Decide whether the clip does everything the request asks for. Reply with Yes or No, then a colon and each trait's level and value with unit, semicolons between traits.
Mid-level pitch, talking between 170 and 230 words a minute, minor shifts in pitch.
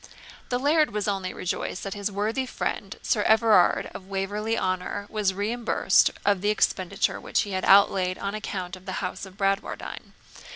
No: high, 200 Hz; average, 175 wpm; narrow, 2.2 semitones